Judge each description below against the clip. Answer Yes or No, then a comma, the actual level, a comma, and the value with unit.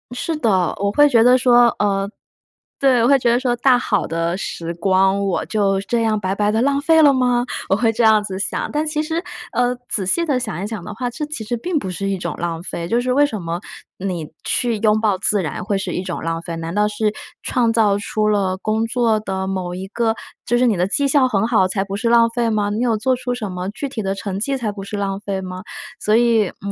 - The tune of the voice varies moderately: Yes, average, 4.0 semitones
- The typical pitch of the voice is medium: No, high, 215 Hz